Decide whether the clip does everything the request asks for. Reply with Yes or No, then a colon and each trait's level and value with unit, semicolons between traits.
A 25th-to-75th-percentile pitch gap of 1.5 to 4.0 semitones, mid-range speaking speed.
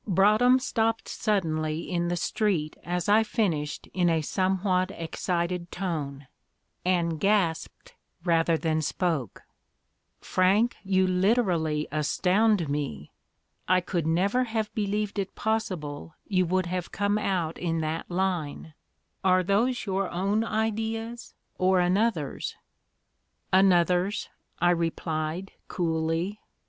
No: average, 3.7 semitones; slow, 110 wpm